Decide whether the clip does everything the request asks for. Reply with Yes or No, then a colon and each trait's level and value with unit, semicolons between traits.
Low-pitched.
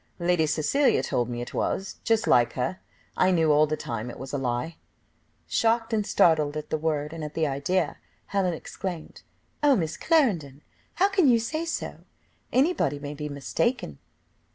No: medium, 160 Hz